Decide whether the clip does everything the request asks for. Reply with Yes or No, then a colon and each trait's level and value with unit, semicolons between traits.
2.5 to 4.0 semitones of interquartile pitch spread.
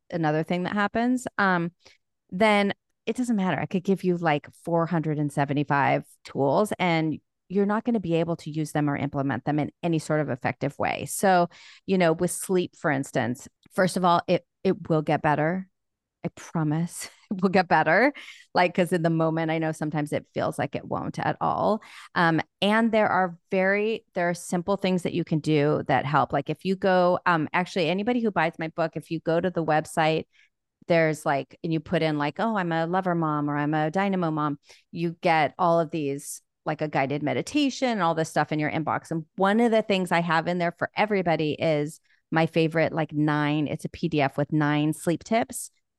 Yes: average, 3.4 semitones